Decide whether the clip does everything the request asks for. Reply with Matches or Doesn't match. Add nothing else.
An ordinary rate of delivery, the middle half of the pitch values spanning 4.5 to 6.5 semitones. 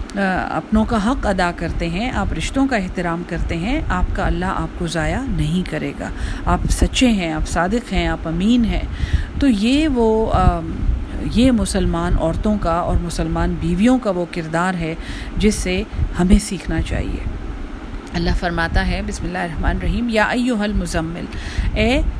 Matches